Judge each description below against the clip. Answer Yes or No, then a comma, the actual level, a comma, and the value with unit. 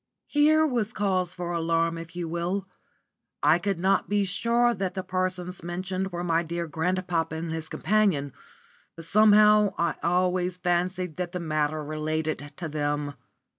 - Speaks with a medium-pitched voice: Yes, medium, 175 Hz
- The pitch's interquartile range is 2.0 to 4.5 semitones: Yes, average, 2.8 semitones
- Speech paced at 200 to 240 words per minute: No, average, 155 wpm